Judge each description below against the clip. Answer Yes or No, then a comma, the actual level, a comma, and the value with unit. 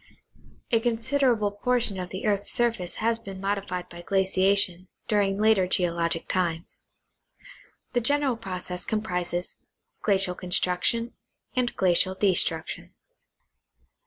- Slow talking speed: Yes, slow, 110 wpm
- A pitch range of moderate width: Yes, average, 3.9 semitones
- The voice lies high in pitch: Yes, high, 195 Hz